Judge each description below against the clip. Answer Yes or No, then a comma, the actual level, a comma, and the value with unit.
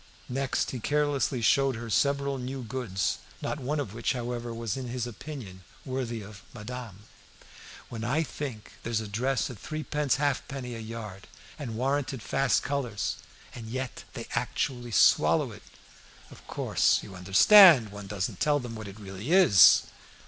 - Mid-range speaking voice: No, low, 125 Hz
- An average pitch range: Yes, average, 3.9 semitones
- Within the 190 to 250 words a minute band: No, average, 160 wpm